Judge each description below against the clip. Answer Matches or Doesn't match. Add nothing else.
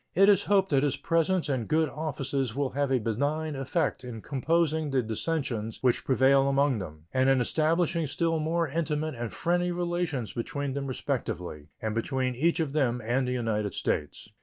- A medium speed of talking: Matches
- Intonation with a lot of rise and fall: Doesn't match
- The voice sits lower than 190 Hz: Matches